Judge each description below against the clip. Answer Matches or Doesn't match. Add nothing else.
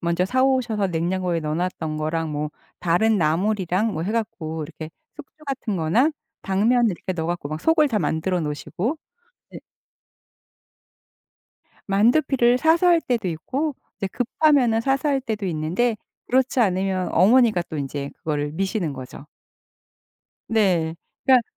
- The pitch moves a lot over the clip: Matches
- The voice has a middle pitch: Doesn't match